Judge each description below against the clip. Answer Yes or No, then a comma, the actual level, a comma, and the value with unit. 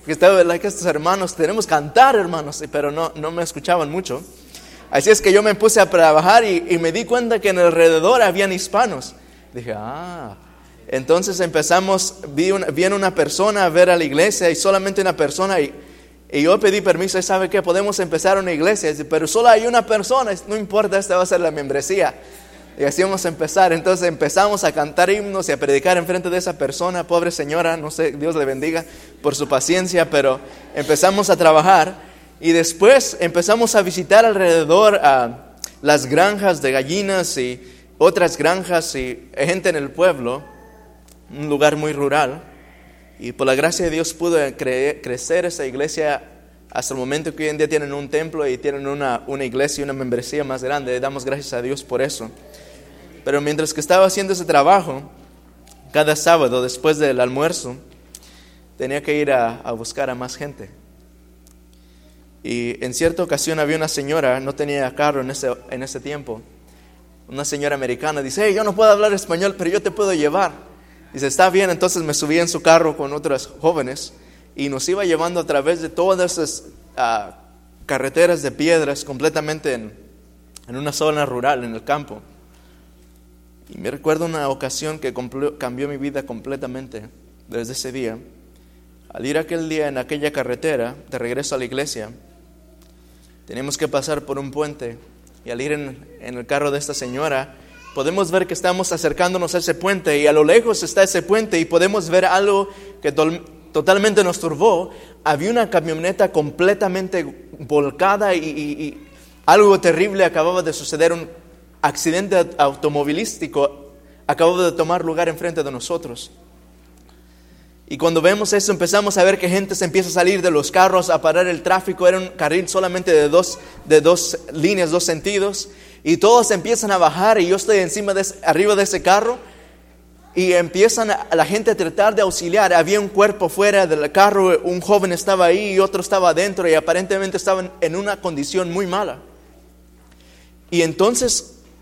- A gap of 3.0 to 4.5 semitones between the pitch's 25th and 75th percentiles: No, wide, 5.4 semitones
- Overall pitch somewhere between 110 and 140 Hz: No, medium, 160 Hz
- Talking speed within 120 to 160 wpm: No, average, 180 wpm